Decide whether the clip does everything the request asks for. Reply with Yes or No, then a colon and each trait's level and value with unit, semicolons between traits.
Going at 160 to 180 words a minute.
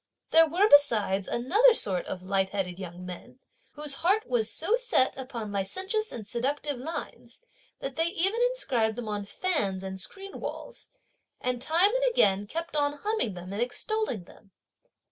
Yes: average, 165 wpm